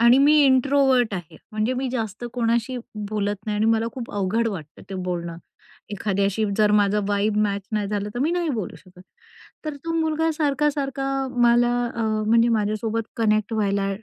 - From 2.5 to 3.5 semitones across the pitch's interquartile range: No, average, 3.9 semitones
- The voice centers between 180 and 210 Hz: No, high, 220 Hz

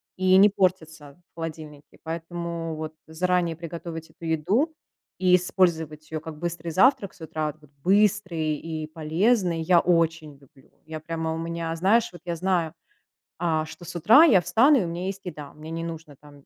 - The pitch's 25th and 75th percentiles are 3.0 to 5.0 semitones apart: No, narrow, 2.5 semitones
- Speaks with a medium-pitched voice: Yes, medium, 165 Hz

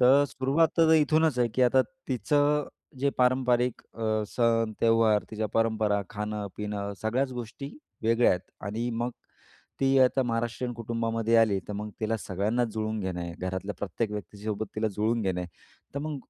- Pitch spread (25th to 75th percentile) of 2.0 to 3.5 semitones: Yes, average, 3.2 semitones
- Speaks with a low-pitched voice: Yes, low, 115 Hz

